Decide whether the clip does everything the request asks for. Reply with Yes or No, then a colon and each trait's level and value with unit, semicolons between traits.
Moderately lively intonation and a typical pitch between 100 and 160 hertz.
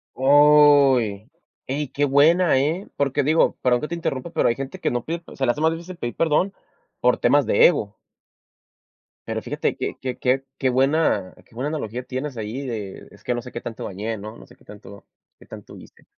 Yes: average, 3.8 semitones; low, 135 Hz